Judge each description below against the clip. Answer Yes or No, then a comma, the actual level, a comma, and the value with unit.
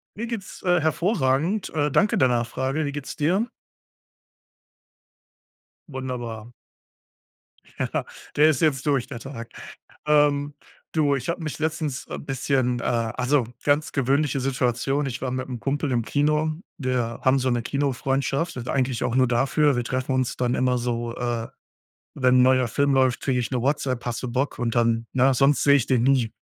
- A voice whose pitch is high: No, low, 130 Hz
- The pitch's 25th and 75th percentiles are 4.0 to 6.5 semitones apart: No, average, 2.9 semitones